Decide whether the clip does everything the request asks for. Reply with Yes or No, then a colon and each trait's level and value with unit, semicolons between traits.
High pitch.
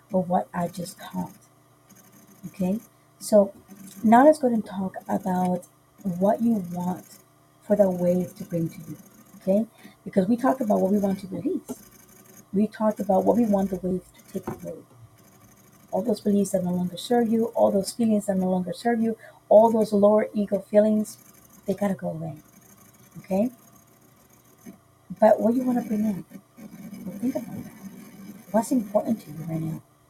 Yes: high, 200 Hz